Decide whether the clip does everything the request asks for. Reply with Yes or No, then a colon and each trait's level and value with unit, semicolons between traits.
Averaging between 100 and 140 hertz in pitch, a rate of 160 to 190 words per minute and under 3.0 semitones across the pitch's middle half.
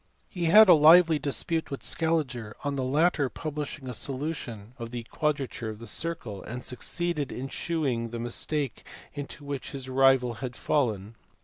No: low, 135 Hz; average, 165 wpm; average, 4.3 semitones